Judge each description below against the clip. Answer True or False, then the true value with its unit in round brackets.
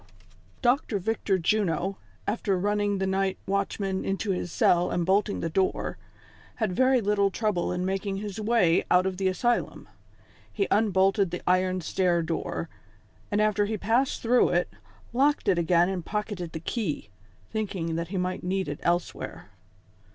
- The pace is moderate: True (160 wpm)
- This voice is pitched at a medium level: False (195 Hz)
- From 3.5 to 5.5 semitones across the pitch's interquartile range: False (2.7 semitones)